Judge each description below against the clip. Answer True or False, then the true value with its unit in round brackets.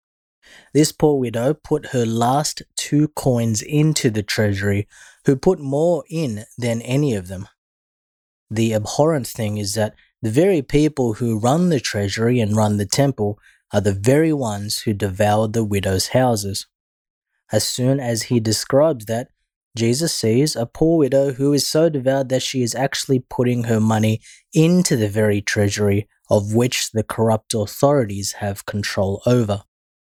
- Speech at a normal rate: True (155 wpm)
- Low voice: True (120 Hz)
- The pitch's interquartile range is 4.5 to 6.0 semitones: True (4.8 semitones)